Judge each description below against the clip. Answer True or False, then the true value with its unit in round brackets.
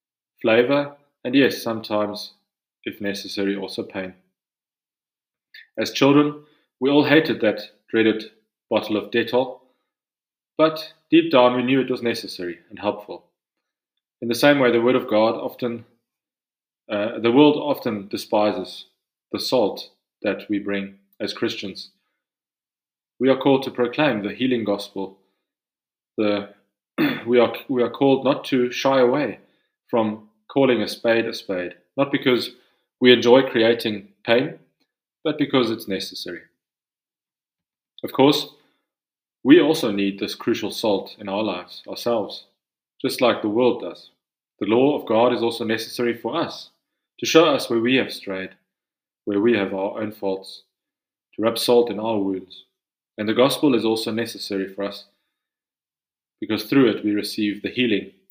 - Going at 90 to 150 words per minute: True (145 wpm)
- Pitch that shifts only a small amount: False (3.7 semitones)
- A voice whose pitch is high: False (115 Hz)